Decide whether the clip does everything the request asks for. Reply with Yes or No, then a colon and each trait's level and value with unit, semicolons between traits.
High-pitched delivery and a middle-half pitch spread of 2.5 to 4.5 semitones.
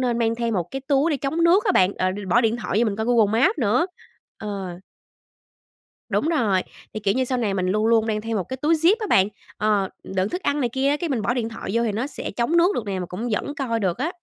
No: high, 230 Hz; average, 5.2 semitones